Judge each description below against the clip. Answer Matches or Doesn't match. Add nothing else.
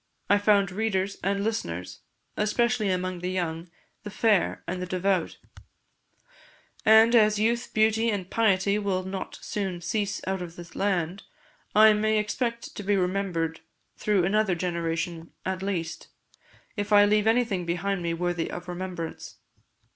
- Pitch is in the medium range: Doesn't match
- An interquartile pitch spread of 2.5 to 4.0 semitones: Matches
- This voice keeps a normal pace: Matches